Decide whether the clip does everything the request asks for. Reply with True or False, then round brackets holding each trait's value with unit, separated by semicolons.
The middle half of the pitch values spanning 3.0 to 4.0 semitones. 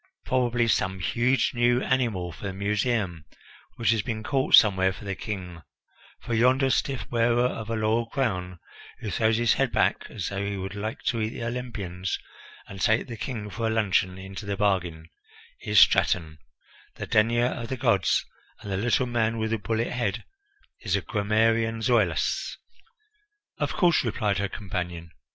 True (3.6 semitones)